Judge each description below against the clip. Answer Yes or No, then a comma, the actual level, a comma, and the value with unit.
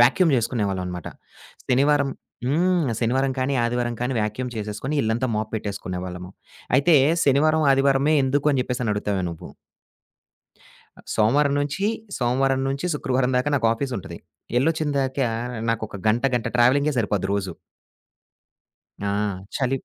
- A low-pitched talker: Yes, low, 130 Hz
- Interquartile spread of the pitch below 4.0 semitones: No, average, 4.4 semitones